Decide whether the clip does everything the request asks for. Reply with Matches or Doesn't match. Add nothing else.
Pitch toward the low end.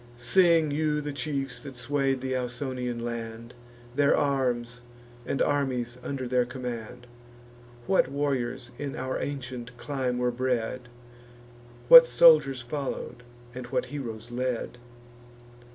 Matches